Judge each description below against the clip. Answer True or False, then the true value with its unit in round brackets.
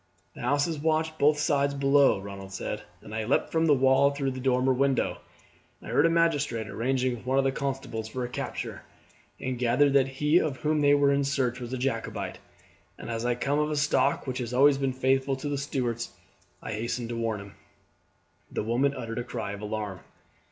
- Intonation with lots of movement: False (3.1 semitones)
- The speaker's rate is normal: False (210 wpm)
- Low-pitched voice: True (130 Hz)